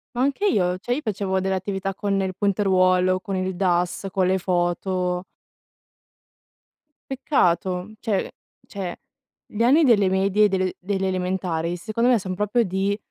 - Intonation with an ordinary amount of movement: No, narrow, 2.1 semitones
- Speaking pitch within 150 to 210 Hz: Yes, high, 190 Hz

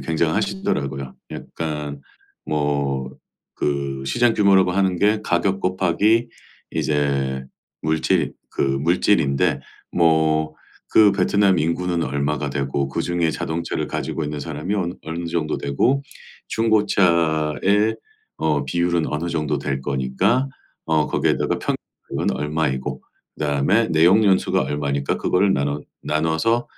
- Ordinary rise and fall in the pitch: Yes, average, 4.6 semitones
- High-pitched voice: No, very low, 80 Hz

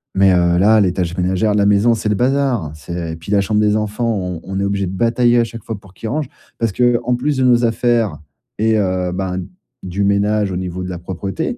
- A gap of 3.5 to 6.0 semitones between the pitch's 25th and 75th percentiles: Yes, average, 3.9 semitones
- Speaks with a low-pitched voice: Yes, low, 100 Hz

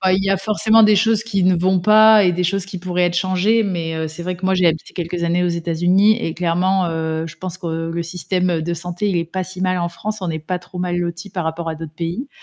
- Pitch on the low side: No, medium, 180 Hz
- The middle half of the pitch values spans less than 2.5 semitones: Yes, narrow, 2.1 semitones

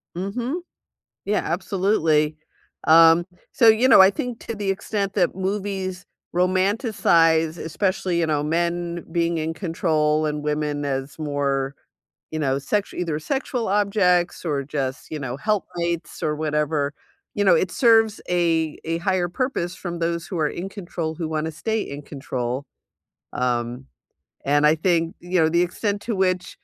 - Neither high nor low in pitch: Yes, medium, 170 Hz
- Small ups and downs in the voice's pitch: No, average, 4.0 semitones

